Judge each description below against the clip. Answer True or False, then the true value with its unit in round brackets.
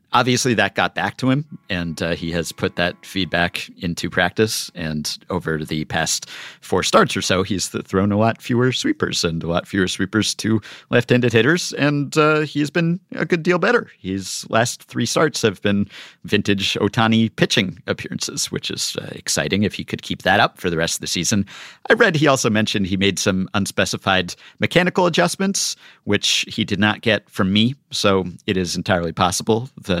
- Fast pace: False (190 wpm)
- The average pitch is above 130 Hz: False (105 Hz)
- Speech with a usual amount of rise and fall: False (5.9 semitones)